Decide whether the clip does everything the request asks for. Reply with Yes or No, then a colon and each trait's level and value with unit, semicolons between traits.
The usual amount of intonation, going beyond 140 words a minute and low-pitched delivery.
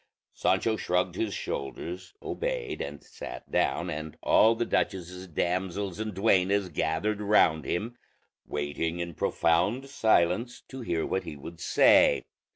No: average, 4.1 semitones; slow, 135 wpm; very low, 90 Hz